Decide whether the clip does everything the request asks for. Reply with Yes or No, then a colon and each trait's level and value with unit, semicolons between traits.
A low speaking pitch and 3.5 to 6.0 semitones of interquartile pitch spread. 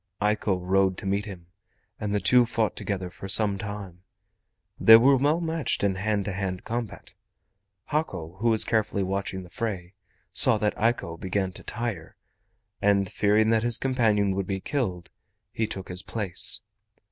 No: low, 100 Hz; average, 3.0 semitones